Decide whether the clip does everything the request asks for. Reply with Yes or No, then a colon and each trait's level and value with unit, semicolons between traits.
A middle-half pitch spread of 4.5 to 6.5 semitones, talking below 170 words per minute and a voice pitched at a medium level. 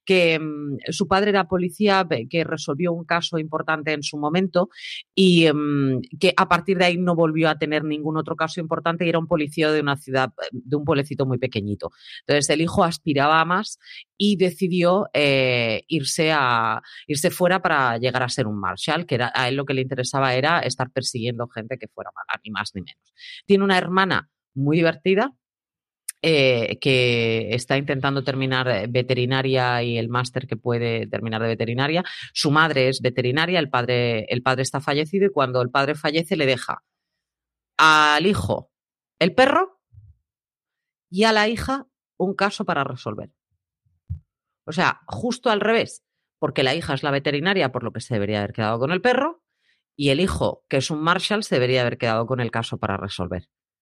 No: wide, 5.6 semitones; average, 185 wpm; medium, 145 Hz